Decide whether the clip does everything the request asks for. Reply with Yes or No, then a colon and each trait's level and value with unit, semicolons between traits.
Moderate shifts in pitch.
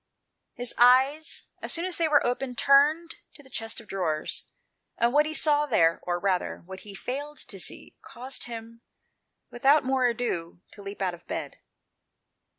No: wide, 6.5 semitones